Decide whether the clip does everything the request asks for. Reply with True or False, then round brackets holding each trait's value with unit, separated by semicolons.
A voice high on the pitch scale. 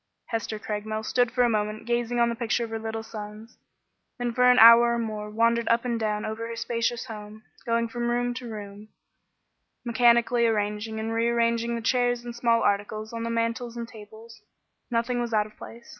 True (230 Hz)